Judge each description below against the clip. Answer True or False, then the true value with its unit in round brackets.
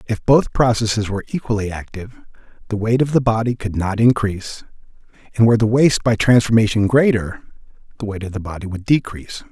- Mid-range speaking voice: False (110 Hz)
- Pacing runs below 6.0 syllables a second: False (6.3 syllables/s)